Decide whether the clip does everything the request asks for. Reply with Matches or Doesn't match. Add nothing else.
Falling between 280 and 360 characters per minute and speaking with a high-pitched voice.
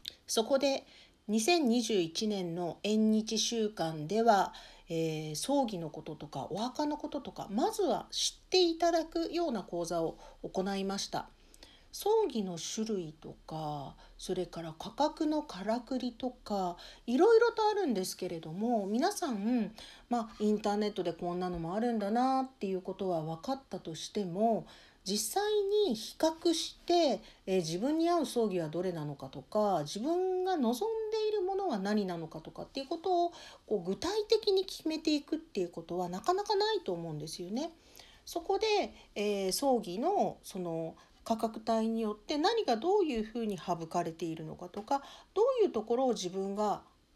Matches